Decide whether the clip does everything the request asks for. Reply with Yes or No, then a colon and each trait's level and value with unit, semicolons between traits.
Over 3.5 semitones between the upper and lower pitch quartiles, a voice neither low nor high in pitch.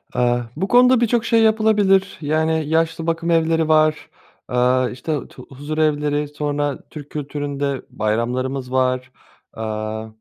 Yes: average, 4.1 semitones; medium, 150 Hz